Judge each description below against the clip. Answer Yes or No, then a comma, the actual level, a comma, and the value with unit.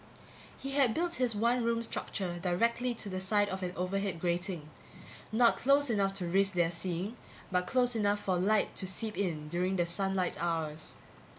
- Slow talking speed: No, average, 185 wpm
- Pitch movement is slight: No, average, 4.4 semitones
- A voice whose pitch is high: Yes, high, 195 Hz